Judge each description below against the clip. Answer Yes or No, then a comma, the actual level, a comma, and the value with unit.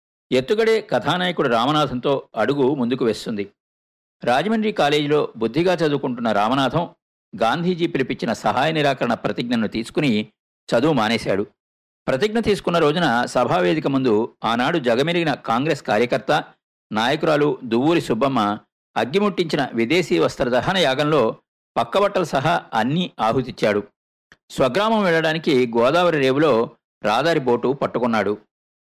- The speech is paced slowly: No, average, 95 wpm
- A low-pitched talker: No, medium, 150 Hz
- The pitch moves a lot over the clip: Yes, wide, 6.9 semitones